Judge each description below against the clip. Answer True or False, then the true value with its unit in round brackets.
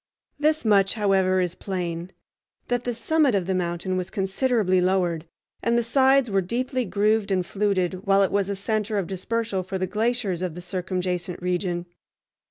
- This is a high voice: True (195 Hz)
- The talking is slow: False (175 wpm)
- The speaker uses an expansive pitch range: False (3.4 semitones)